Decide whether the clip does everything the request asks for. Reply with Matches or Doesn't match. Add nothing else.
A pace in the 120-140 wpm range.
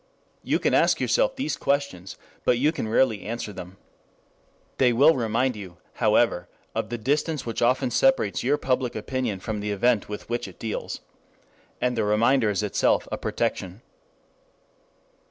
Doesn't match